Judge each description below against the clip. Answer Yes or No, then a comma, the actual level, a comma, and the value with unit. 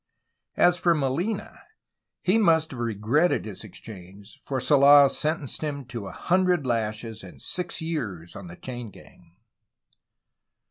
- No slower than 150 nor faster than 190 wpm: No, slow, 135 wpm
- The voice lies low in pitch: Yes, low, 130 Hz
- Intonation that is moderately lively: No, wide, 7.2 semitones